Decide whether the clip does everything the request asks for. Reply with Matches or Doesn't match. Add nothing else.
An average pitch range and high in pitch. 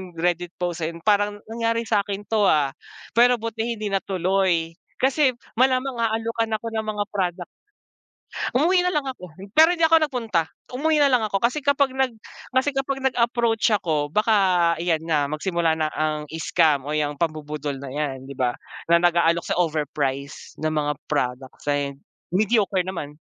Doesn't match